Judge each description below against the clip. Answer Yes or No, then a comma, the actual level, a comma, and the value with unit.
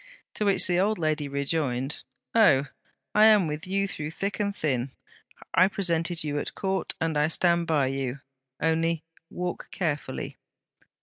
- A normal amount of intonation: Yes, average, 4.4 semitones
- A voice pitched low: No, medium, 165 Hz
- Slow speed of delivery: No, average, 150 wpm